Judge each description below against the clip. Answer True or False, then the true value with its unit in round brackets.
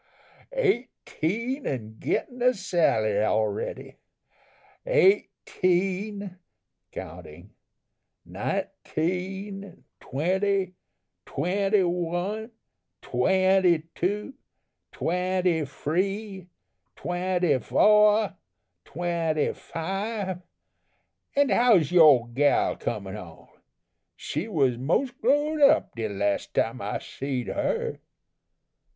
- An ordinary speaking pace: False (75 wpm)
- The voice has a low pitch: False (185 Hz)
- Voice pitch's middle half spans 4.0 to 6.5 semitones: True (5.2 semitones)